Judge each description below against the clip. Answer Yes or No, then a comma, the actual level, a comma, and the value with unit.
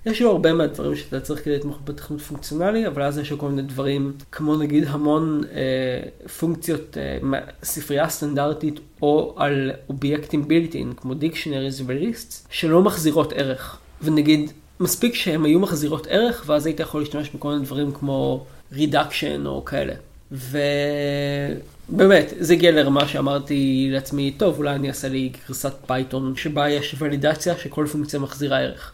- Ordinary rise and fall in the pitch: No, narrow, 2.1 semitones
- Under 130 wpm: No, fast, 150 wpm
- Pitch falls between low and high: Yes, medium, 145 Hz